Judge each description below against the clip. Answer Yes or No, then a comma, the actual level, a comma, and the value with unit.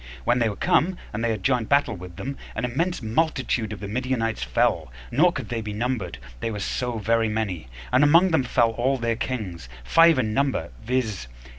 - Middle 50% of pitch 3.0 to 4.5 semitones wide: Yes, average, 3.6 semitones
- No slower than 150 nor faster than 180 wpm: No, average, 200 wpm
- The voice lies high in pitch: No, low, 115 Hz